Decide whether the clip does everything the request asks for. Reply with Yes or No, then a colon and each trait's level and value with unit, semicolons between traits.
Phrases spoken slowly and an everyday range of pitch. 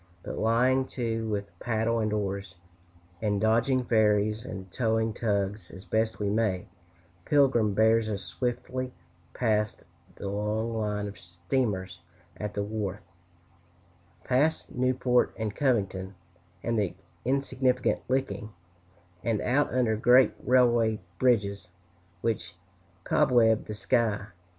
Yes: slow, 115 wpm; average, 3.2 semitones